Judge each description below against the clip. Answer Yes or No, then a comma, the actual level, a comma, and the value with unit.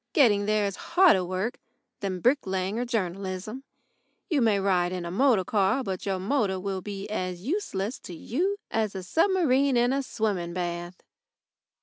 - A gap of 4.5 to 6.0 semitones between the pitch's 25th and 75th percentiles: Yes, average, 5.2 semitones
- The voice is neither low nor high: No, high, 200 Hz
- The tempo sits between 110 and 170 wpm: Yes, average, 160 wpm